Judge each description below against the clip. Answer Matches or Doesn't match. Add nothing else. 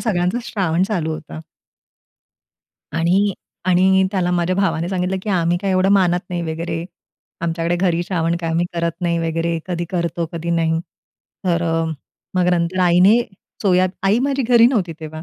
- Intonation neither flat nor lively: Doesn't match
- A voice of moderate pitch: Matches